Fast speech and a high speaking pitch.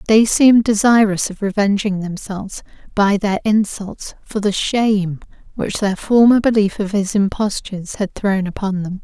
No: average, 155 wpm; high, 205 Hz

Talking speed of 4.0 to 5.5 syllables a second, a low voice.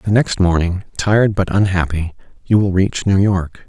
Yes: 4.8 syllables/s; very low, 95 Hz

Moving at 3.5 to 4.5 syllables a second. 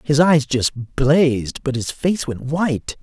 Yes: 3.8 syllables/s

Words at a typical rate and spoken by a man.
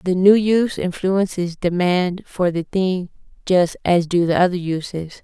No: average, 160 wpm; female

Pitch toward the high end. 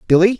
Yes: high, 195 Hz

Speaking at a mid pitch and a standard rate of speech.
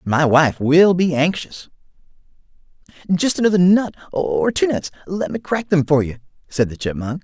Yes: medium, 165 Hz; average, 160 wpm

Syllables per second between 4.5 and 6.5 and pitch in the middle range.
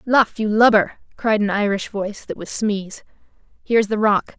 No: 5.0 syllables/s; high, 210 Hz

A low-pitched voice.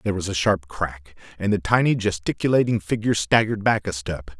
Yes: low, 100 Hz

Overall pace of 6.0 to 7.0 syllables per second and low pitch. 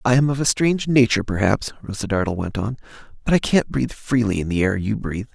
Yes: 6.5 syllables/s; low, 115 Hz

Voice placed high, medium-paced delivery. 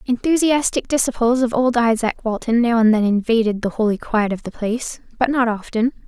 Yes: high, 235 Hz; average, 190 wpm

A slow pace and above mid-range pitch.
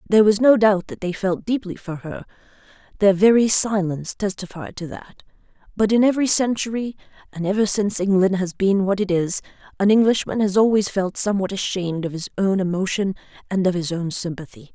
No: average, 180 wpm; high, 195 Hz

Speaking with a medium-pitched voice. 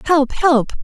No: very high, 290 Hz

